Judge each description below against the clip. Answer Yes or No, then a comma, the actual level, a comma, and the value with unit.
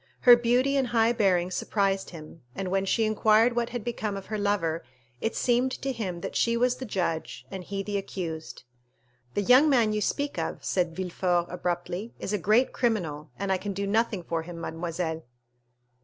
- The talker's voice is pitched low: No, high, 200 Hz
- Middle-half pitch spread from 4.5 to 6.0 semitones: Yes, average, 4.8 semitones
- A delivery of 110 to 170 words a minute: No, average, 190 wpm